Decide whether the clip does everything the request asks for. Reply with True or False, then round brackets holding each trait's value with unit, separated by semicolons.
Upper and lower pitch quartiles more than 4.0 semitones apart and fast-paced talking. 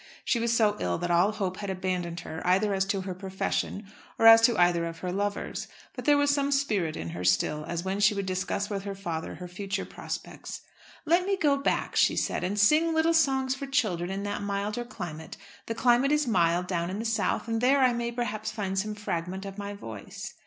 True (4.7 semitones; 225 wpm)